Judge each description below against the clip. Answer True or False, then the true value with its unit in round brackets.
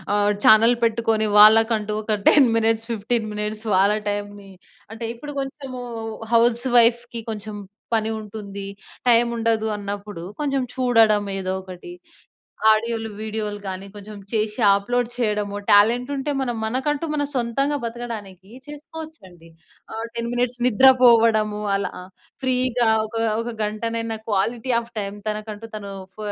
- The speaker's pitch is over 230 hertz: False (225 Hz)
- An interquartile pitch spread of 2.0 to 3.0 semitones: True (2.6 semitones)